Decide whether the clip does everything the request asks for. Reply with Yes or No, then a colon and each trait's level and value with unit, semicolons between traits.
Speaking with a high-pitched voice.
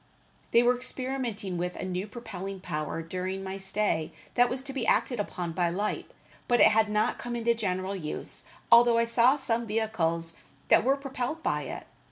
Yes: high, 215 Hz